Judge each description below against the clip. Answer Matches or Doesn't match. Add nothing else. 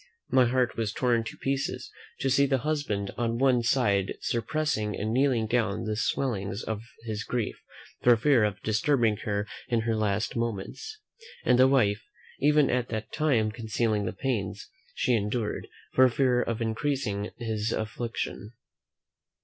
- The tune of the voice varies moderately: Matches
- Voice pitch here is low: Matches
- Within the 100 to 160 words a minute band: Matches